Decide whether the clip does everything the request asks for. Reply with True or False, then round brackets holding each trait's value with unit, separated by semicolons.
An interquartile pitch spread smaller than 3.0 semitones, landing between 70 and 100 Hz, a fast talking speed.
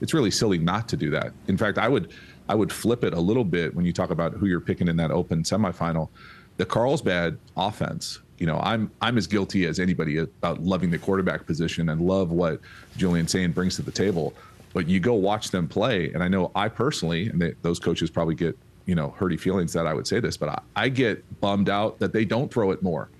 True (2.4 semitones; 90 Hz; 240 wpm)